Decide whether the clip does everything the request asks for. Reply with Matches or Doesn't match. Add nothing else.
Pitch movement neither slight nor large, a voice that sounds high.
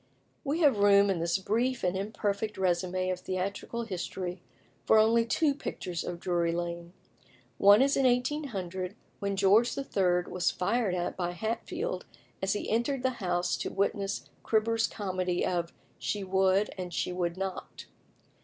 Matches